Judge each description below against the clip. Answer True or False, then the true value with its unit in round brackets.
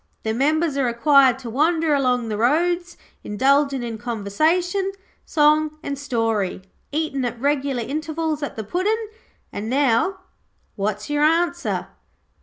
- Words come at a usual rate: False (130 wpm)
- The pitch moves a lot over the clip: False (5.0 semitones)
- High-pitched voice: True (280 Hz)